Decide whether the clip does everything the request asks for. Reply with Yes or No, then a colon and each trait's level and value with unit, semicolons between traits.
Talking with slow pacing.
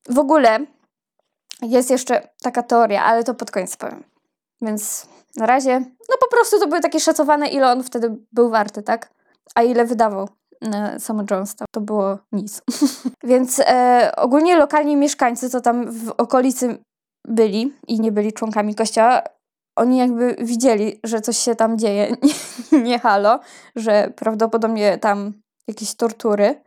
No: average, 150 wpm